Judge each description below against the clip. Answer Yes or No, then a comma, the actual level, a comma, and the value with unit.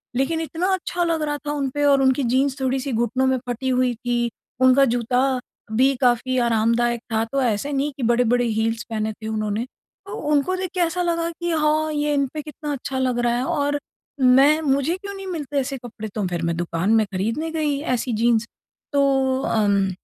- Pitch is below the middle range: No, very high, 260 Hz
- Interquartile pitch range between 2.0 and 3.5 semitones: No, average, 4.0 semitones